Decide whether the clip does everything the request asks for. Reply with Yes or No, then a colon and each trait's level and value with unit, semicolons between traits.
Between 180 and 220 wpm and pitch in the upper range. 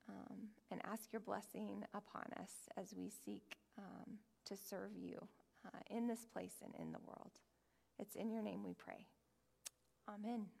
No: average, 165 wpm; high, 225 Hz